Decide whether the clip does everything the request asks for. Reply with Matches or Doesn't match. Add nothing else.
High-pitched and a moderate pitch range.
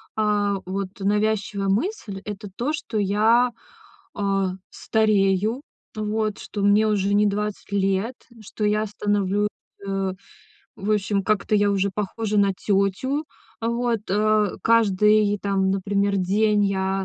Doesn't match